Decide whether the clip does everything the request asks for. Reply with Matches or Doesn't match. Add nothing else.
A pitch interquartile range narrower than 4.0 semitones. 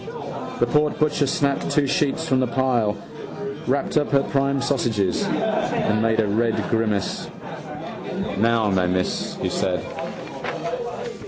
Doesn't match